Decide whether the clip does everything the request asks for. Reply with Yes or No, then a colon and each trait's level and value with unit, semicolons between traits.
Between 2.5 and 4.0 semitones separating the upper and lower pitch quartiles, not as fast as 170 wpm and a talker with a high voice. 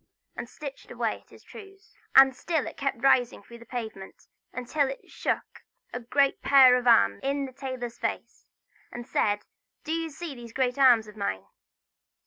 No: average, 2.9 semitones; average, 175 wpm; very high, 255 Hz